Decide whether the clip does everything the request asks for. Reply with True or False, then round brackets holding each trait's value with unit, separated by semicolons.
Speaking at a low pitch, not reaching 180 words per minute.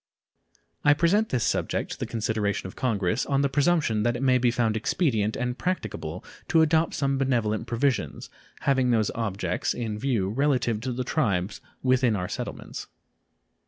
True (120 Hz; 160 wpm)